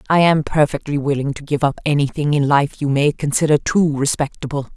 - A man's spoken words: No, female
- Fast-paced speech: No, average, 190 wpm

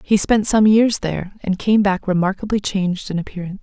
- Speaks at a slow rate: No, average, 200 wpm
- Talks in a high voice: Yes, high, 200 Hz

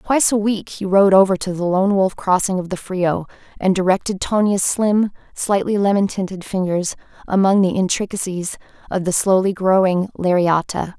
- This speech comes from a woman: Yes, female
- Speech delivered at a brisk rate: No, average, 165 wpm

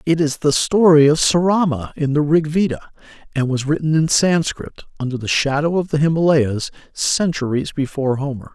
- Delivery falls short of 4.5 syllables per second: No, 5.2 syllables/s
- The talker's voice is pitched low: No, medium, 150 Hz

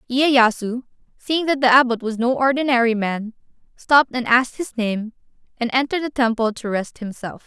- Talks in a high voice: Yes, high, 245 Hz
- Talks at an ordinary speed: Yes, average, 170 wpm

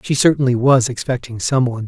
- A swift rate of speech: No, average, 195 wpm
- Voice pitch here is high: No, low, 125 Hz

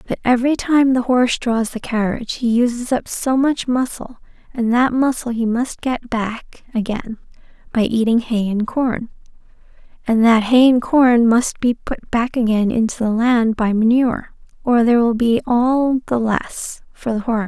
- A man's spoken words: No, female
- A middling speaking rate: Yes, average, 185 wpm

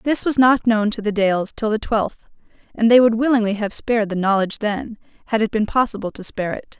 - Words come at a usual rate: No, fast, 230 wpm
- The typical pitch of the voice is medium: No, high, 220 Hz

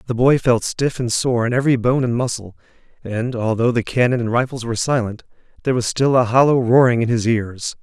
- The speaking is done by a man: Yes, male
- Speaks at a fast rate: Yes, fast, 215 wpm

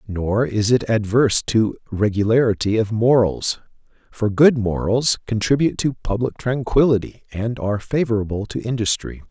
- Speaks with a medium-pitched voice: No, low, 115 Hz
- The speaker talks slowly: Yes, slow, 130 wpm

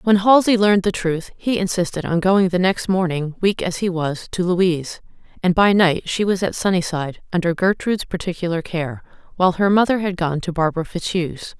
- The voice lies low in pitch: No, medium, 180 Hz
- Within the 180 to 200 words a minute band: Yes, average, 190 wpm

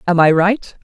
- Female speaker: Yes, female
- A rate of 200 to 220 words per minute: Yes, fast, 215 wpm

